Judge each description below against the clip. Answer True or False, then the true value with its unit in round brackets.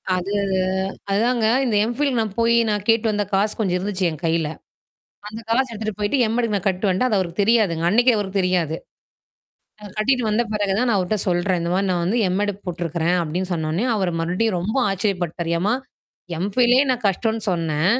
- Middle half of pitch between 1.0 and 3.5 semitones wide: False (3.9 semitones)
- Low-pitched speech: False (200 Hz)